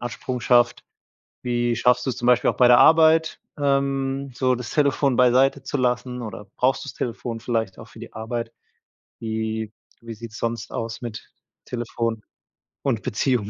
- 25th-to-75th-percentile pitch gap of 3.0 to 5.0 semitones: No, narrow, 2.5 semitones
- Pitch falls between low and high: No, low, 120 Hz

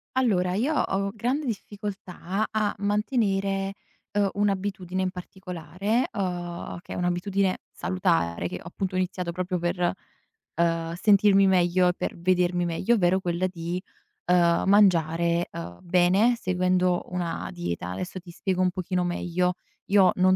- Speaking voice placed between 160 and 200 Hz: Yes, medium, 185 Hz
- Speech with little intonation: Yes, narrow, 2.1 semitones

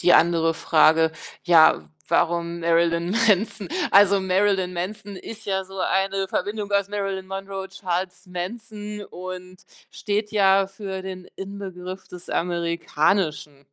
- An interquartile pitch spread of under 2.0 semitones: No, narrow, 2.4 semitones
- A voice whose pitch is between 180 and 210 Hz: Yes, high, 190 Hz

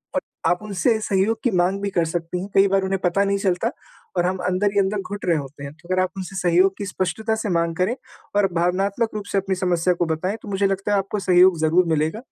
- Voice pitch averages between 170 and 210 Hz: Yes, high, 190 Hz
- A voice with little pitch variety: Yes, narrow, 2.2 semitones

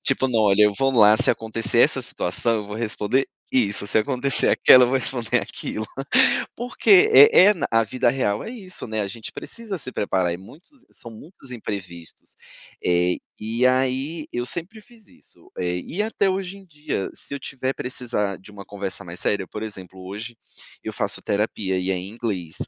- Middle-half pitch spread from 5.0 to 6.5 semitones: Yes, average, 5.3 semitones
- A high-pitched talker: No, low, 115 Hz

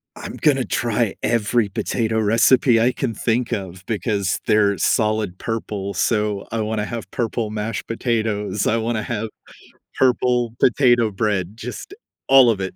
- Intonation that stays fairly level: Yes, narrow, 2.2 semitones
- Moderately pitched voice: No, low, 110 Hz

